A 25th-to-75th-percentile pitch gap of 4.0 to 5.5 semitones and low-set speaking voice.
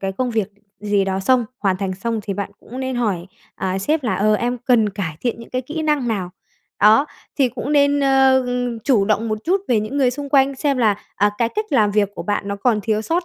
No: average, 4.4 semitones; high, 230 Hz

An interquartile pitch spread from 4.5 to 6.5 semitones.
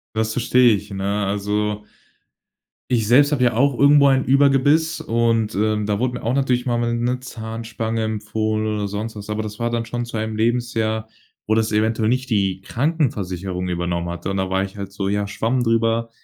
No: average, 2.8 semitones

